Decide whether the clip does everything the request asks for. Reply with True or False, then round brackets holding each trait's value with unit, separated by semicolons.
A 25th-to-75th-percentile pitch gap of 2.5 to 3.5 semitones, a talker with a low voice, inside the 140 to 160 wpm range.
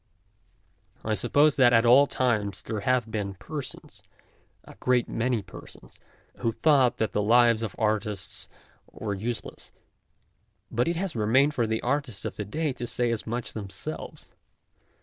True (3.1 semitones; 115 Hz; 155 wpm)